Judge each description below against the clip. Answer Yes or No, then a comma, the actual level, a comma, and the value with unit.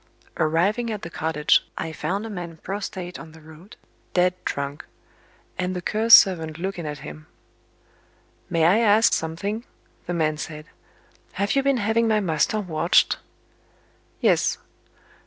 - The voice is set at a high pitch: No, medium, 180 Hz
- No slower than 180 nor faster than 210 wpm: No, average, 140 wpm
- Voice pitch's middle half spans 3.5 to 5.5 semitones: Yes, average, 4.6 semitones